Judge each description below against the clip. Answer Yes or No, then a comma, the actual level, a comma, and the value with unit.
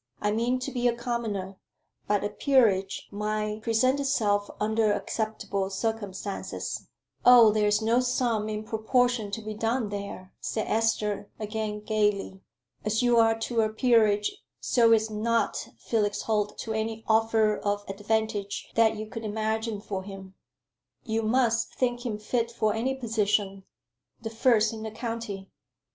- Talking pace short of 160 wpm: Yes, average, 150 wpm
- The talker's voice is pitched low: No, high, 220 Hz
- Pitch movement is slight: Yes, narrow, 1.8 semitones